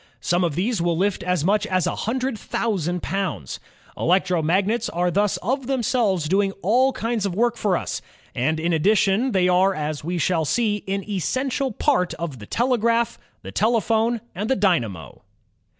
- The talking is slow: No, average, 175 wpm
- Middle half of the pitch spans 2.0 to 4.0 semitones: No, average, 4.7 semitones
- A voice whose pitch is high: Yes, high, 195 Hz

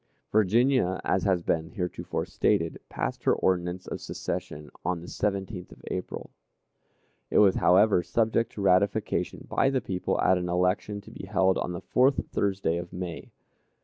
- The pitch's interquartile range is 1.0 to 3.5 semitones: Yes, average, 2.8 semitones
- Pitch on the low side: Yes, very low, 95 Hz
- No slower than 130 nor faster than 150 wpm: No, average, 160 wpm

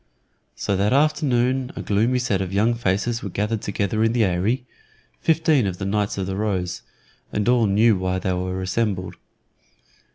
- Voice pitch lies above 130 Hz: No, low, 105 Hz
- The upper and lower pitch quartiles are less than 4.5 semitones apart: Yes, average, 3.9 semitones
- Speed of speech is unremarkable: Yes, average, 170 wpm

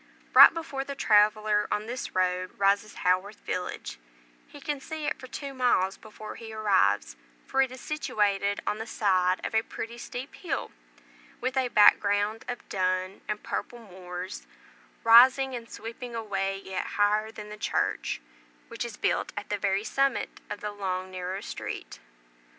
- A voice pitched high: Yes, high, 210 Hz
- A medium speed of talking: Yes, average, 165 wpm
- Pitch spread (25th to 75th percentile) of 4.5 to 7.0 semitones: No, average, 3.9 semitones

